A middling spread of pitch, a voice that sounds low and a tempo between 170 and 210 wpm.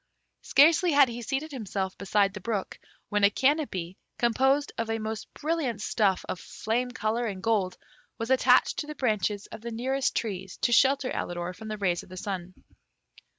No: average, 5.0 semitones; high, 225 Hz; average, 180 wpm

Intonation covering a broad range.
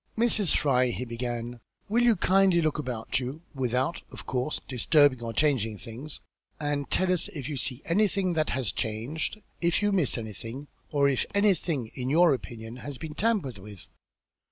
Yes: wide, 5.9 semitones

